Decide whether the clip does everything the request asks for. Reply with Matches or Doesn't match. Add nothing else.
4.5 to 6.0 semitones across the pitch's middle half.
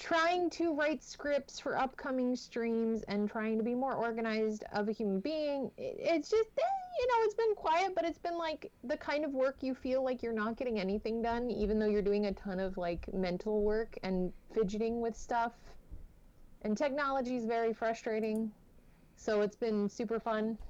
Matches